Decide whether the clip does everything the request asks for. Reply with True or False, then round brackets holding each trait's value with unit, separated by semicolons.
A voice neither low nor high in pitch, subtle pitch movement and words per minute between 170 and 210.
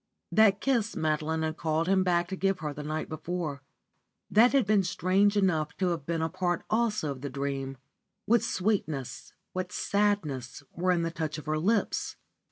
False (175 Hz; 4.6 semitones; 180 wpm)